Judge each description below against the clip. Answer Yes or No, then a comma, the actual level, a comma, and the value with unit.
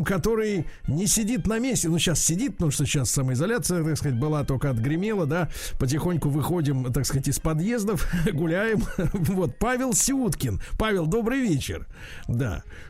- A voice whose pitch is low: No, medium, 165 Hz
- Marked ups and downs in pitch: Yes, wide, 6.9 semitones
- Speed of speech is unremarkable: Yes, average, 150 wpm